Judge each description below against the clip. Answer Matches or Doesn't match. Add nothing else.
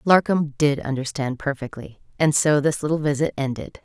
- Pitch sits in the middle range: Matches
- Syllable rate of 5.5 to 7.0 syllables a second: Doesn't match